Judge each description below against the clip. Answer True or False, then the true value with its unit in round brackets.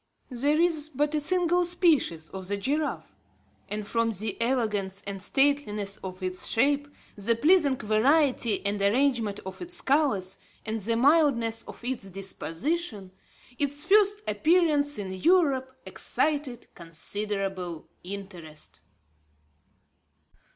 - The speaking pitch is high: True (235 Hz)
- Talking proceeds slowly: True (115 wpm)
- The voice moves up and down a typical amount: False (6.8 semitones)